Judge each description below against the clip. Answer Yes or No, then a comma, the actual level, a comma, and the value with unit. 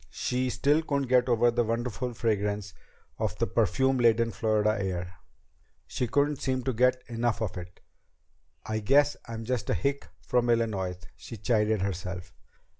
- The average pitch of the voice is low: Yes, low, 115 Hz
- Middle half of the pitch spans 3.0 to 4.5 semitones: Yes, average, 3.3 semitones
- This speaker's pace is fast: No, average, 155 wpm